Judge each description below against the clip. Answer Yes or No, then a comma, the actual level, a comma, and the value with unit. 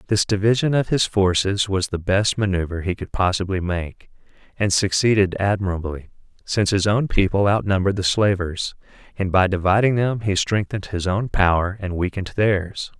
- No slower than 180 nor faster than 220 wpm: No, average, 160 wpm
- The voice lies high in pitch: No, very low, 95 Hz